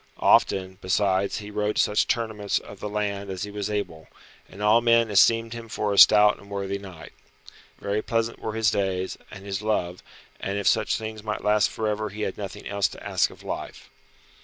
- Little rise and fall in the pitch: Yes, narrow, 1.5 semitones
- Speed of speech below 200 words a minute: No, fast, 205 wpm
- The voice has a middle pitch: No, low, 105 Hz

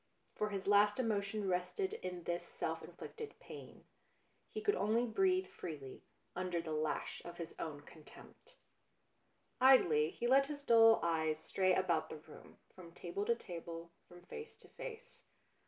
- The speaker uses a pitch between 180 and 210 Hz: Yes, high, 190 Hz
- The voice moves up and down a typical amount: No, wide, 7.1 semitones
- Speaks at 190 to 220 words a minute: No, average, 155 wpm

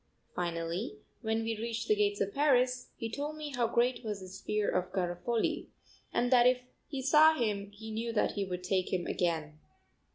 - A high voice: Yes, high, 220 Hz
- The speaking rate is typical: Yes, average, 190 wpm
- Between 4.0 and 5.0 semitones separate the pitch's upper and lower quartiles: Yes, average, 4.7 semitones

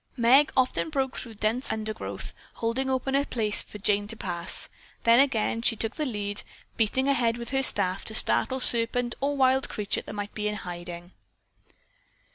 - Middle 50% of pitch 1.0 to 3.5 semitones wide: No, average, 3.9 semitones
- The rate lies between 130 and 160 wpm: No, average, 175 wpm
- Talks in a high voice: Yes, high, 230 Hz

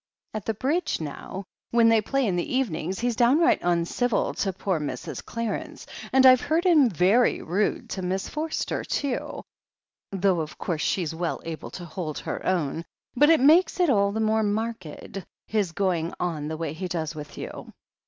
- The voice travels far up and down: Yes, wide, 6.3 semitones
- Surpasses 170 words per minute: Yes, average, 180 wpm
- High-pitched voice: Yes, high, 195 Hz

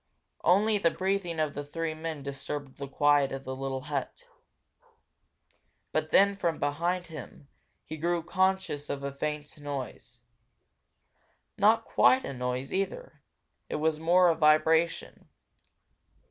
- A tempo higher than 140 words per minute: No, slow, 135 wpm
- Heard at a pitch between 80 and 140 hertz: No, medium, 155 Hz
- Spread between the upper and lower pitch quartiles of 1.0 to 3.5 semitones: No, average, 4.0 semitones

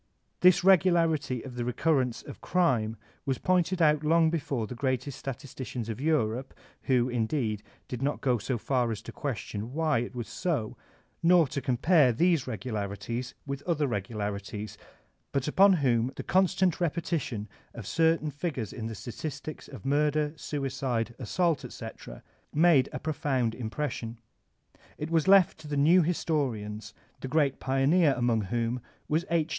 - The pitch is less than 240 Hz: Yes, low, 135 Hz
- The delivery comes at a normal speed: Yes, average, 155 wpm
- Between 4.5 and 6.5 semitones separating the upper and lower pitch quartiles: Yes, average, 5.1 semitones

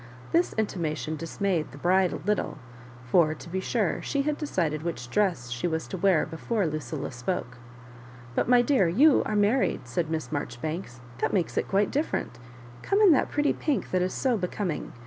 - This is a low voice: No, medium, 180 Hz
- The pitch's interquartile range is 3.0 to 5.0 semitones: No, wide, 5.5 semitones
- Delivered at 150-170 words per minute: No, average, 185 wpm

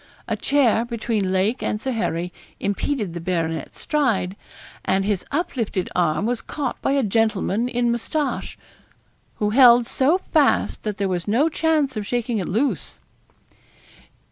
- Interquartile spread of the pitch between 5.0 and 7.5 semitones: Yes, average, 5.3 semitones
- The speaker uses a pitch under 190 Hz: No, high, 225 Hz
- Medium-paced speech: Yes, average, 145 wpm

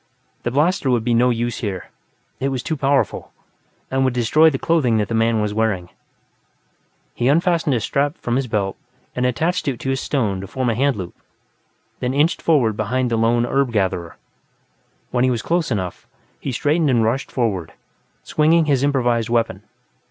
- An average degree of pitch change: Yes, average, 3.7 semitones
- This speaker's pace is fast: No, average, 180 wpm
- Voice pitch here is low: Yes, low, 125 Hz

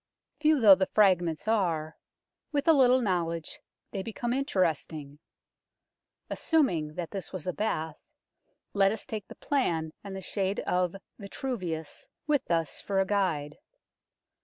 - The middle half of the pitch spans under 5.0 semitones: No, average, 5.3 semitones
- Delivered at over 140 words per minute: No, slow, 135 wpm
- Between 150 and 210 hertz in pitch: Yes, high, 190 Hz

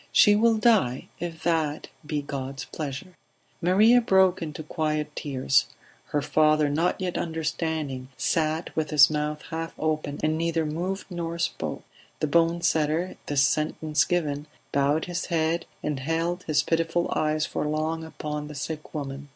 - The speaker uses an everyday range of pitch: No, narrow, 2.2 semitones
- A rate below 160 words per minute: Yes, average, 150 wpm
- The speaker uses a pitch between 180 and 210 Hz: No, medium, 155 Hz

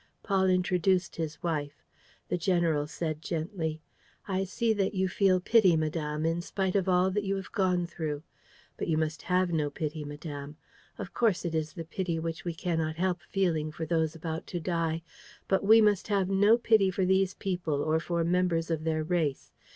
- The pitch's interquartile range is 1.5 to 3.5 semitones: Yes, average, 3.1 semitones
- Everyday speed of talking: Yes, average, 190 wpm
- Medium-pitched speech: Yes, medium, 170 Hz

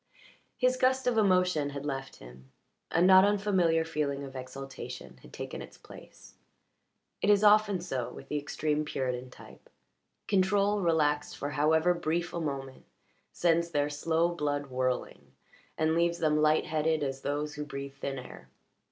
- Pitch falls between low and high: Yes, medium, 155 Hz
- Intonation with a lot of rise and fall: No, average, 4.0 semitones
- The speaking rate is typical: Yes, average, 155 wpm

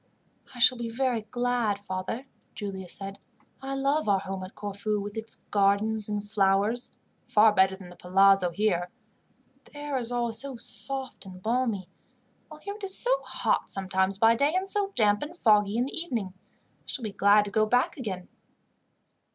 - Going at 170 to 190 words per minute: Yes, average, 175 wpm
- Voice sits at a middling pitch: No, high, 215 Hz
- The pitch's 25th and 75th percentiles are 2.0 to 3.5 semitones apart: No, average, 4.0 semitones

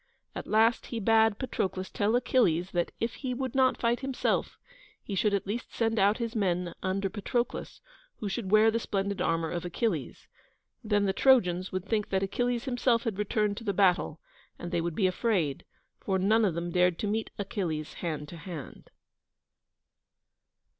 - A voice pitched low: No, high, 200 Hz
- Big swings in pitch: No, average, 4.0 semitones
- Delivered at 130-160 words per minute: No, average, 175 wpm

